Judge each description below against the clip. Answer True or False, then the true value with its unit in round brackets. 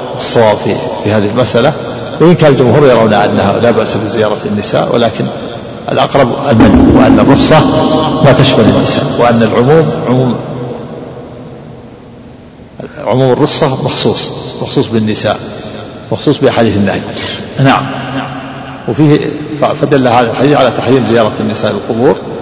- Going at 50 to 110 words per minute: False (120 wpm)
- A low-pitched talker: True (125 Hz)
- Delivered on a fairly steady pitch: False (4.8 semitones)